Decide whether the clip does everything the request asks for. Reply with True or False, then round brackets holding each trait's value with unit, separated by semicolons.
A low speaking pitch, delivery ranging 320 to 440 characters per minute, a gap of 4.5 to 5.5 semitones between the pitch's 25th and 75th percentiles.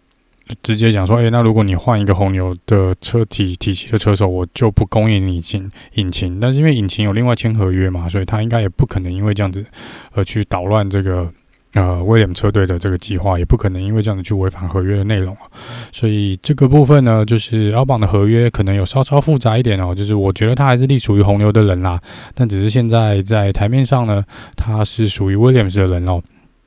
False (105 Hz; 350 characters per minute; 3.1 semitones)